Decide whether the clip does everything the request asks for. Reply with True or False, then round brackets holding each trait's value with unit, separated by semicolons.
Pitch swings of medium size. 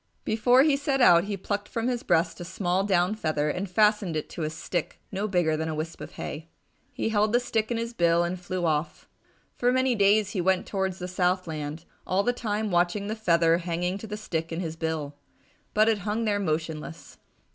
True (4.2 semitones)